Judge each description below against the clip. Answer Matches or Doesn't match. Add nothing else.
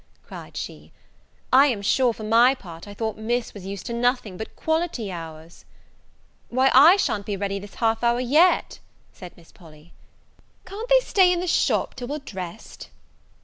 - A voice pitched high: Matches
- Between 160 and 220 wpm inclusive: Matches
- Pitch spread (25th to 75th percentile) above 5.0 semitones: Matches